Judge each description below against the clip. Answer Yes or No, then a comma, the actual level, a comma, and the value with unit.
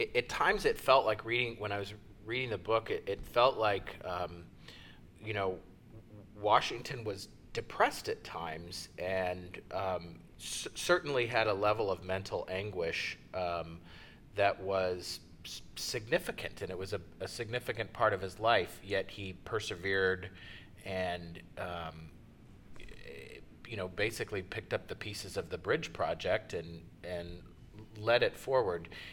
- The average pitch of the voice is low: Yes, very low, 95 Hz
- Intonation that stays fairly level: No, average, 3.8 semitones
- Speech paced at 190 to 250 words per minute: No, average, 140 wpm